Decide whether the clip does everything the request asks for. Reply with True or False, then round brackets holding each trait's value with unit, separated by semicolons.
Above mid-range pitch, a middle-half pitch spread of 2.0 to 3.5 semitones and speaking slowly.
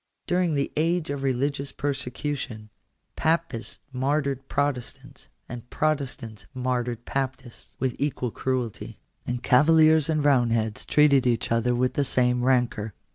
False (130 Hz; 2.9 semitones; 130 wpm)